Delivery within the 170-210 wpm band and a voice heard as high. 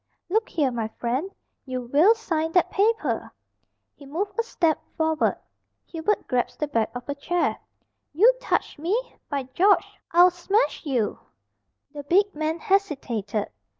No: average, 145 wpm; very high, 320 Hz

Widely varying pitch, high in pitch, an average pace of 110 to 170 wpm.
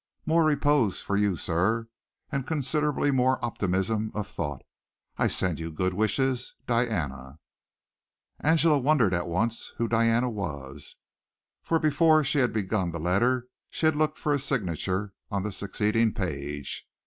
No: wide, 6.8 semitones; low, 110 Hz; average, 145 wpm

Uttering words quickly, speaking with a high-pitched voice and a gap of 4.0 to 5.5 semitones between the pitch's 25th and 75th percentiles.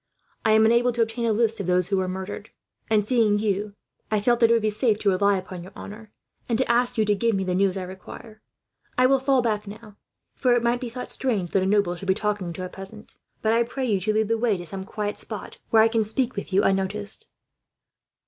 No: fast, 255 wpm; high, 215 Hz; average, 3.0 semitones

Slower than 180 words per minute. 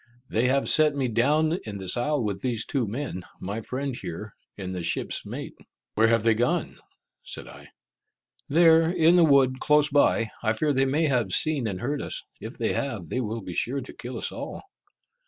No: average, 200 wpm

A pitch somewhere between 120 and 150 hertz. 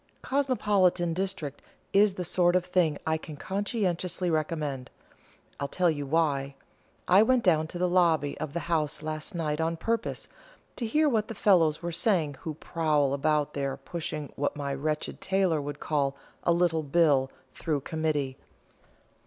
No: medium, 160 Hz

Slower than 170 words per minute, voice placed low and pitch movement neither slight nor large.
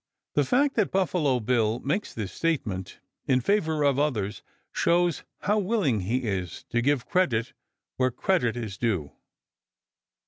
No: average, 140 wpm; low, 130 Hz; wide, 7.7 semitones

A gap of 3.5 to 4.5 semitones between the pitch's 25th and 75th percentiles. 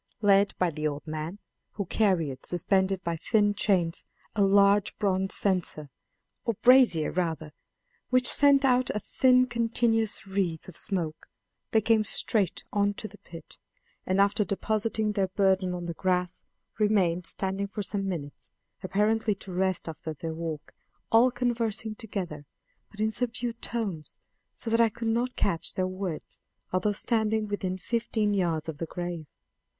Yes: average, 3.9 semitones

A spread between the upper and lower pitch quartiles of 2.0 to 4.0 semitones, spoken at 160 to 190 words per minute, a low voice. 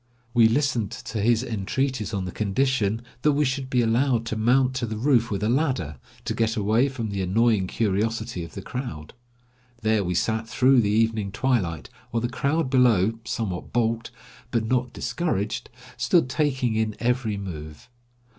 Yes: average, 3.5 semitones; average, 170 wpm; low, 115 Hz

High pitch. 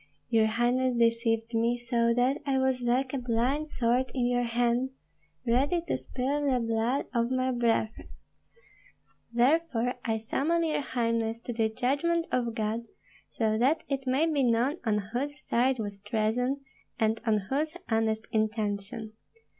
Yes: high, 240 Hz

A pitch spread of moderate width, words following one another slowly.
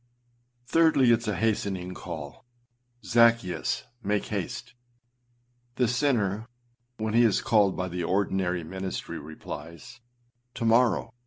Yes: average, 4.4 semitones; slow, 125 wpm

